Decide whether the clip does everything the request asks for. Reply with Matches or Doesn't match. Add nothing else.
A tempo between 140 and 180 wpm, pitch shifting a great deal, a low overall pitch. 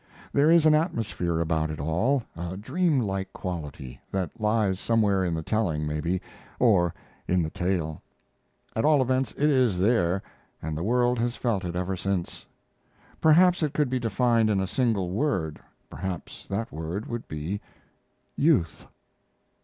Matches